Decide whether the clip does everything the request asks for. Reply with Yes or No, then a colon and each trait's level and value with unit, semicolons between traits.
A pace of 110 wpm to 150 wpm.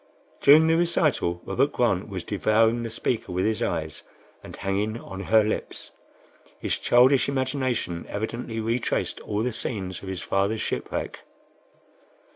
Yes: average, 140 wpm